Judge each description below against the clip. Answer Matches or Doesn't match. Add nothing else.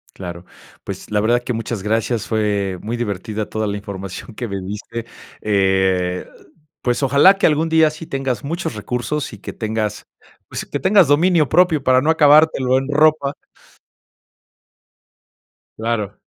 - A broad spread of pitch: Matches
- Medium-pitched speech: Doesn't match